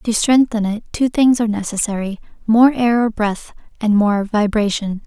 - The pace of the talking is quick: No, average, 165 wpm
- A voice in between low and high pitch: No, high, 220 Hz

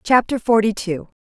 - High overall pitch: Yes, high, 215 Hz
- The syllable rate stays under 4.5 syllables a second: No, 5.0 syllables/s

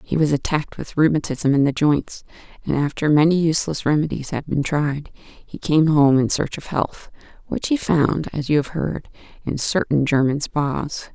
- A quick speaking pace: No, average, 185 wpm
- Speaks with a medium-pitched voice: Yes, medium, 150 Hz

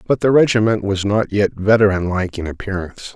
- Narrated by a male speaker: Yes, male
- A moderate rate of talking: Yes, average, 170 wpm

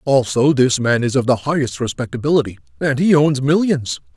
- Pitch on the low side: Yes, low, 130 Hz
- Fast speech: No, average, 175 wpm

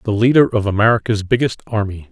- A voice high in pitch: No, low, 110 Hz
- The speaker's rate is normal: Yes, average, 170 wpm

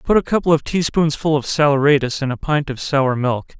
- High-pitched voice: No, medium, 145 Hz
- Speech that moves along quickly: Yes, fast, 235 wpm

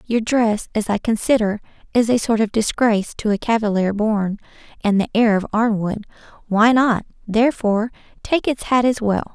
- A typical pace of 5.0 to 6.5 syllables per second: Yes, 5.1 syllables/s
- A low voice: No, high, 220 Hz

